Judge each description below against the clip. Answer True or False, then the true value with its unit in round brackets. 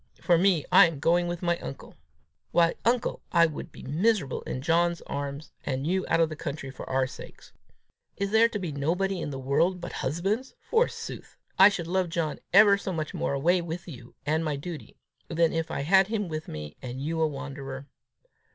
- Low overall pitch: False (165 Hz)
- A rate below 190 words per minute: False (205 wpm)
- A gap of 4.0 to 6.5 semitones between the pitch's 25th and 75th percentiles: True (4.4 semitones)